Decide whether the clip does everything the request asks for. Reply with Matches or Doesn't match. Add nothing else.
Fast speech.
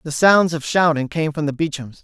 Matches